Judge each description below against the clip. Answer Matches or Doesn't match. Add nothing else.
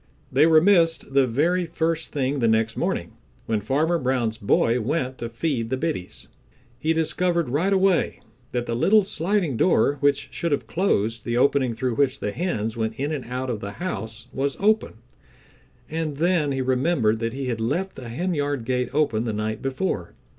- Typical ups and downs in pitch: Doesn't match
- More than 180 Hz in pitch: Doesn't match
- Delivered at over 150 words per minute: Matches